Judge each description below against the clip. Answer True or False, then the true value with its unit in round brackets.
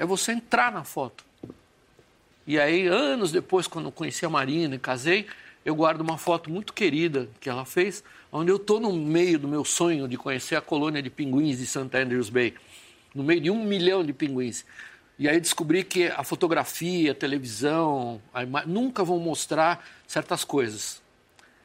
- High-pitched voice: False (160 Hz)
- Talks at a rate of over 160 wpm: True (180 wpm)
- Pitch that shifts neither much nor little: True (4.7 semitones)